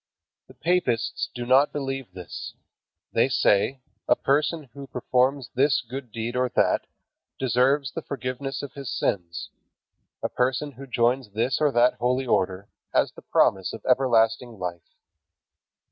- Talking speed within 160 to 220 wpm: No, average, 145 wpm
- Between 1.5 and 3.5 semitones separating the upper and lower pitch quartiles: Yes, average, 2.8 semitones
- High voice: No, low, 125 Hz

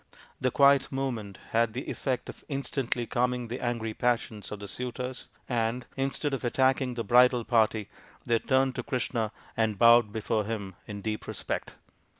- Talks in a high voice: No, low, 120 Hz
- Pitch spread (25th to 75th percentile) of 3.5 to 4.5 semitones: No, narrow, 2.6 semitones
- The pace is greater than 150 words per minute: Yes, average, 160 wpm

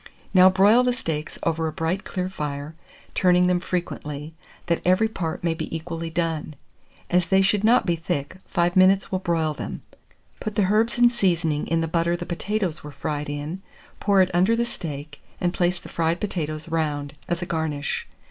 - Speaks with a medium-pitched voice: Yes, medium, 170 Hz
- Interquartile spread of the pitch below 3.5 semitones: Yes, average, 2.9 semitones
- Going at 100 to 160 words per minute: No, average, 185 wpm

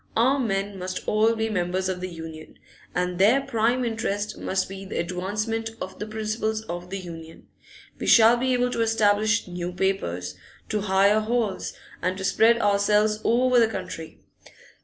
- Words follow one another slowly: No, average, 165 wpm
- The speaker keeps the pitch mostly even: No, average, 3.4 semitones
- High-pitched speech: Yes, high, 205 Hz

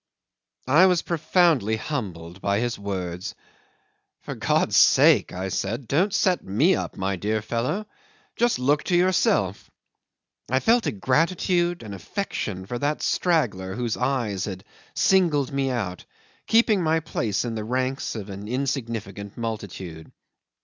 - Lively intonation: Yes, wide, 8.3 semitones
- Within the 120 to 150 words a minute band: Yes, average, 140 wpm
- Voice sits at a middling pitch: No, low, 120 Hz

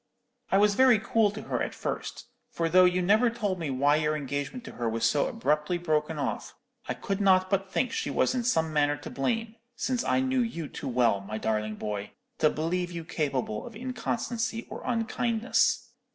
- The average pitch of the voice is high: No, medium, 180 Hz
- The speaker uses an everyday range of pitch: No, wide, 7.8 semitones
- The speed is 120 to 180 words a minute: No, average, 195 wpm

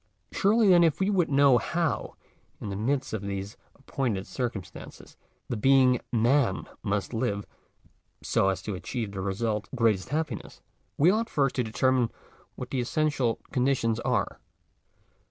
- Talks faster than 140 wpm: No, slow, 135 wpm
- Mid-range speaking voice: No, low, 125 Hz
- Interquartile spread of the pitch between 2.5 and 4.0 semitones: No, average, 5.2 semitones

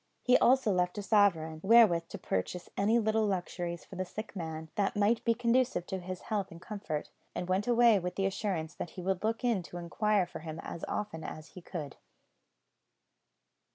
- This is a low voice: No, high, 190 Hz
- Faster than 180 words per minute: Yes, average, 190 wpm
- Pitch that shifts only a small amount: No, average, 4.0 semitones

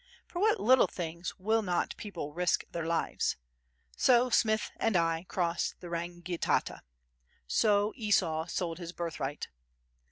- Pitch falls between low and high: Yes, medium, 175 Hz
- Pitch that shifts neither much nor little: Yes, average, 4.2 semitones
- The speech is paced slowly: Yes, slow, 130 wpm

